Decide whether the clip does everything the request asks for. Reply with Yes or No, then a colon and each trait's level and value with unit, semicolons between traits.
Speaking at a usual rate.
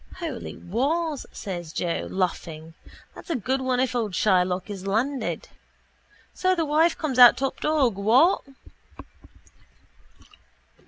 No: slow, 120 wpm